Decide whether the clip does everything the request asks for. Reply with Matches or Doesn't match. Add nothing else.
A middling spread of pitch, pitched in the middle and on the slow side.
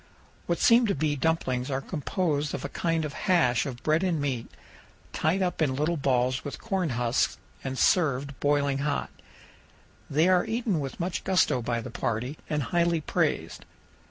Doesn't match